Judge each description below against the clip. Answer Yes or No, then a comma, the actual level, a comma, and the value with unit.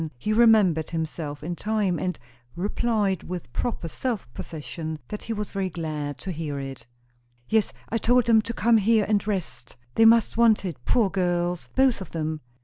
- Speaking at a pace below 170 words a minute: No, average, 175 wpm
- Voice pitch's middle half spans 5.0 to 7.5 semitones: Yes, wide, 5.6 semitones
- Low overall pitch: No, high, 190 Hz